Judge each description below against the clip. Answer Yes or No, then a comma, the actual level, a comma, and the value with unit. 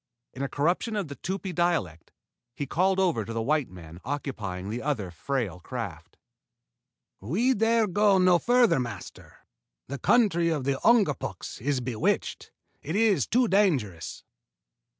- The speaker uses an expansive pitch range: Yes, wide, 9.0 semitones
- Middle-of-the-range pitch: Yes, medium, 145 Hz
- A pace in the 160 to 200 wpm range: No, average, 145 wpm